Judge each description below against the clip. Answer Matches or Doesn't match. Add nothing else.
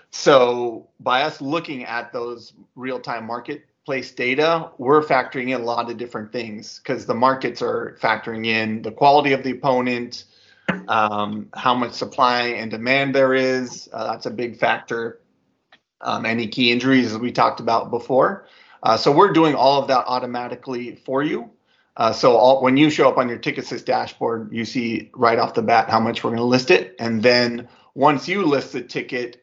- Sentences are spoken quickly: Doesn't match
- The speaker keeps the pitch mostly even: Matches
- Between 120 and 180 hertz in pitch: Matches